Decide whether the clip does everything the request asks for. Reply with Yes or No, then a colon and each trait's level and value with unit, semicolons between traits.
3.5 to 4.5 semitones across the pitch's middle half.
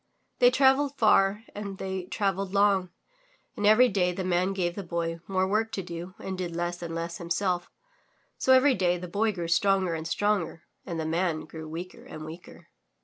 No: average, 2.9 semitones